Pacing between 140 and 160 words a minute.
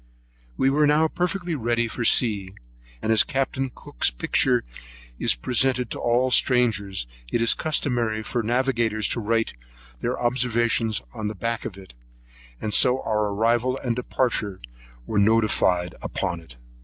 Yes: average, 145 wpm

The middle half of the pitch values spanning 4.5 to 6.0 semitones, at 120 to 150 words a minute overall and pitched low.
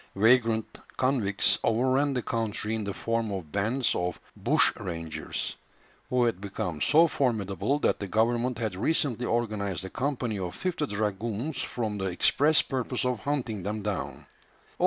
No: average, 4.0 semitones; average, 145 wpm; low, 110 Hz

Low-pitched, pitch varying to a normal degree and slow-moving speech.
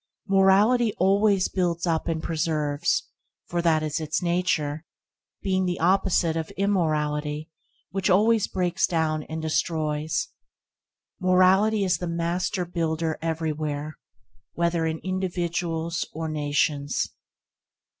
No: medium, 170 Hz; average, 3.0 semitones; slow, 105 wpm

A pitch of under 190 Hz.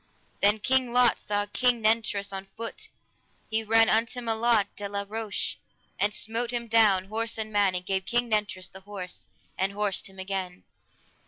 No: high, 210 Hz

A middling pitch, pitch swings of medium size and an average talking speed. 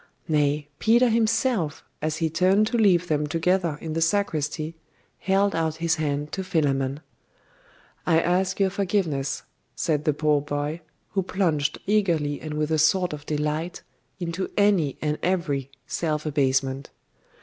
Yes: medium, 160 Hz; average, 4.0 semitones; average, 145 wpm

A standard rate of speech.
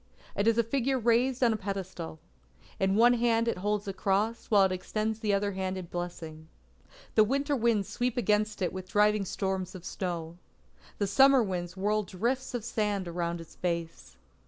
Yes: average, 180 wpm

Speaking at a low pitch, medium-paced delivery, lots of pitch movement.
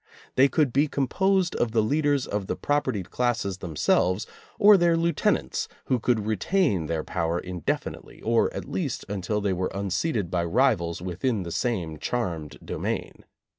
Yes: low, 110 Hz; average, 155 wpm; wide, 7.4 semitones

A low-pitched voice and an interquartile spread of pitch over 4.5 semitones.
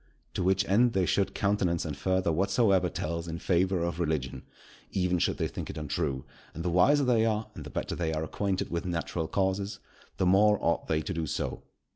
No: very low, 90 Hz; average, 2.9 semitones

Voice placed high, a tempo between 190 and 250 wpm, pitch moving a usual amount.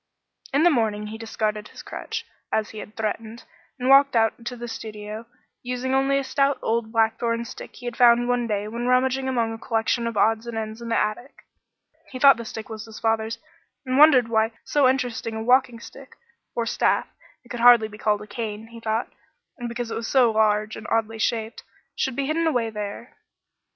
No: high, 230 Hz; average, 200 wpm; narrow, 2.2 semitones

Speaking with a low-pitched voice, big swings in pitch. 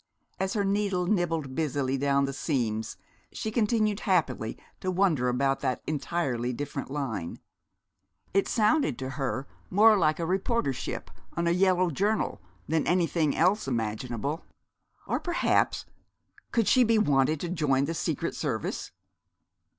No: medium, 160 Hz; wide, 6.3 semitones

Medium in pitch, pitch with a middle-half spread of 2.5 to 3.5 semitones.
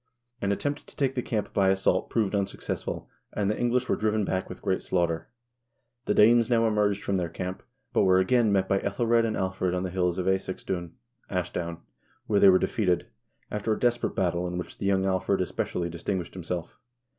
No: very low, 95 Hz; average, 2.9 semitones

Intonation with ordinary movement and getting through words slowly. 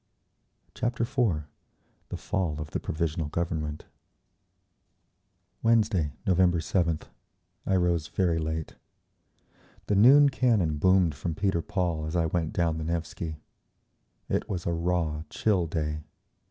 Yes: average, 3.2 semitones; slow, 125 wpm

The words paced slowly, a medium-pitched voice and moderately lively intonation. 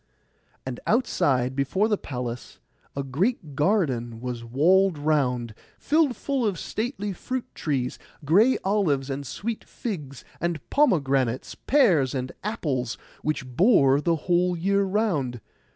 No: slow, 125 wpm; medium, 155 Hz; wide, 7.7 semitones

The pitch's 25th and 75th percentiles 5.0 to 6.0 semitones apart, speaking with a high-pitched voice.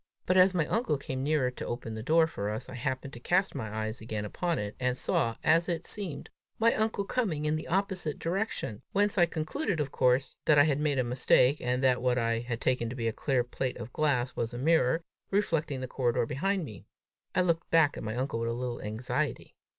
No: wide, 5.5 semitones; low, 135 Hz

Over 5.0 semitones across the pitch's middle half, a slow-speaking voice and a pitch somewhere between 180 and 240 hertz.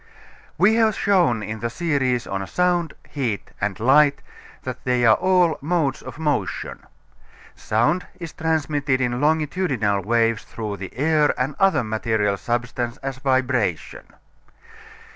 No: wide, 5.6 semitones; slow, 125 wpm; low, 130 Hz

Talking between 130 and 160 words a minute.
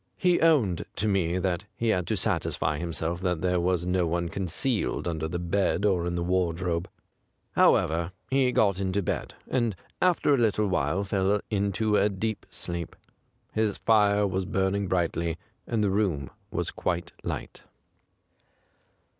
Yes: average, 155 wpm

